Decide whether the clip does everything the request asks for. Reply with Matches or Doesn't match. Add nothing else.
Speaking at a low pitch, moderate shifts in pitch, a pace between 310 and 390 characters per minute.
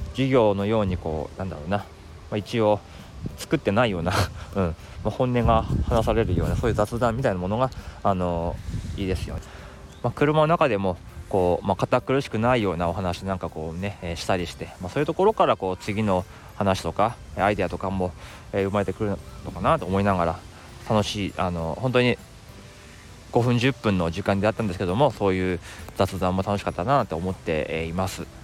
Matches